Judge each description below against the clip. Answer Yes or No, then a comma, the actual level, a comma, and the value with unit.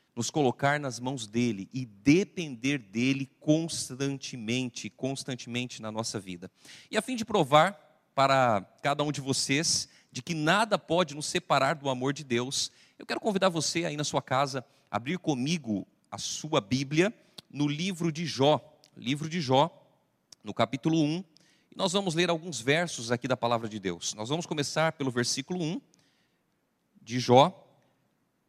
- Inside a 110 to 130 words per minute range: No, average, 160 wpm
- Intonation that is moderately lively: Yes, average, 4.6 semitones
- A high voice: No, medium, 140 Hz